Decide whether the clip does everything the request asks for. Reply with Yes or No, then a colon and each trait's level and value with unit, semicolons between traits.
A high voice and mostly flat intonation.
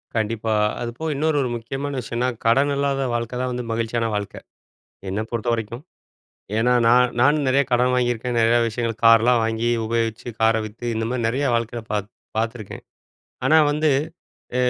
No: low, 120 Hz; narrow, 2.0 semitones